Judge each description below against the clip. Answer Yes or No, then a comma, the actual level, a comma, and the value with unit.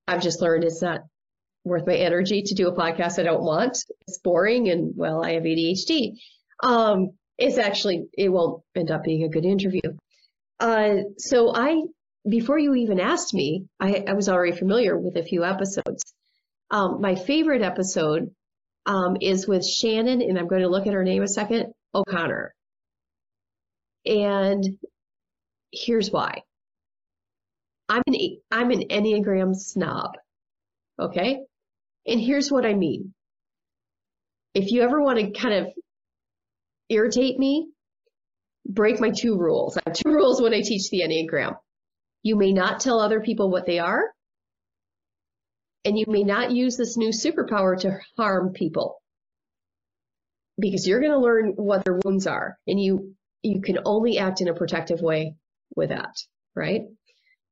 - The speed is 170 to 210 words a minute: No, average, 155 wpm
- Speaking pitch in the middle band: No, high, 195 Hz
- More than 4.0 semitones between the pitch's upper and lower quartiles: Yes, average, 4.5 semitones